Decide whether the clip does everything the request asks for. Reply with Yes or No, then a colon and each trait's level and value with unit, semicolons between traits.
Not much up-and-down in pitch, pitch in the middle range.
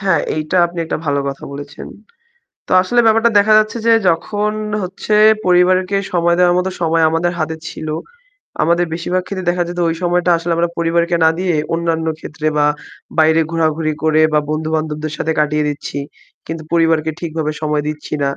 Yes: narrow, 2.3 semitones; medium, 165 Hz